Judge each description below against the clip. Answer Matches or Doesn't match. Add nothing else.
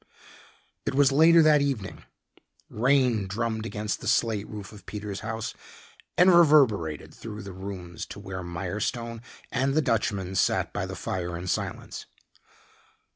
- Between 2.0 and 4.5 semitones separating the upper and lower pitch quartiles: Doesn't match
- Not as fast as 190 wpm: Matches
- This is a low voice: Matches